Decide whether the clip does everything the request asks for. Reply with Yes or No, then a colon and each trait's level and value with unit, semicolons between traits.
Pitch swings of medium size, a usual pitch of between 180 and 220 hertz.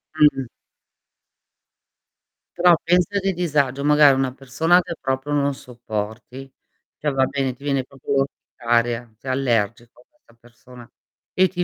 No: average, 3.3 semitones; low, 135 Hz